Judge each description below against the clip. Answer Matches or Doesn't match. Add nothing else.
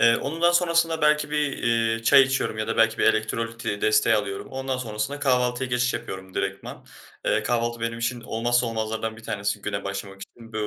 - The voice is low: Matches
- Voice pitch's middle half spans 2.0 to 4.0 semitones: Matches